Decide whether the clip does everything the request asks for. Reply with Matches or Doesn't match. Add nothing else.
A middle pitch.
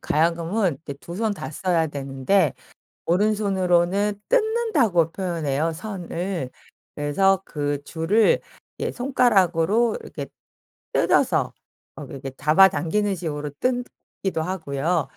Matches